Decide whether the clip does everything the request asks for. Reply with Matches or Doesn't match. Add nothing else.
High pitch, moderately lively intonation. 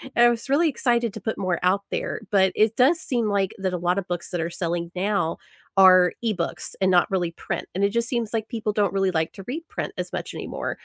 Matches